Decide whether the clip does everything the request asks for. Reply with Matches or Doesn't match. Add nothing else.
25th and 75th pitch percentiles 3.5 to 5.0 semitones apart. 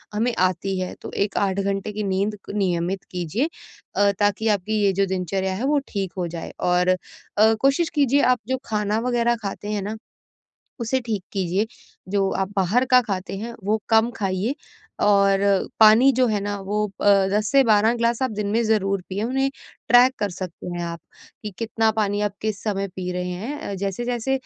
Doesn't match